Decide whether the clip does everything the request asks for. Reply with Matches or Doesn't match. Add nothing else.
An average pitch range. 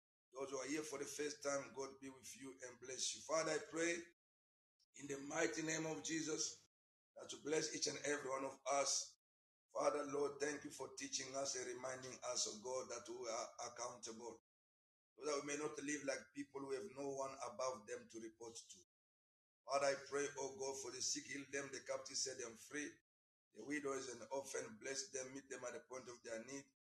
Doesn't match